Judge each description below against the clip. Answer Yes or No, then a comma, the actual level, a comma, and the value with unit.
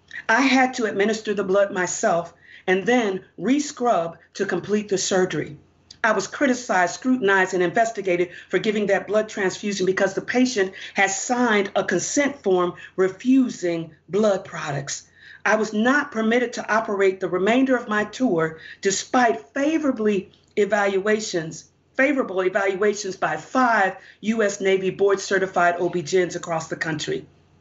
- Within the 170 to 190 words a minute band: No, slow, 135 wpm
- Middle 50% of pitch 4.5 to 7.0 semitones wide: No, average, 3.2 semitones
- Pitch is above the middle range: Yes, high, 195 Hz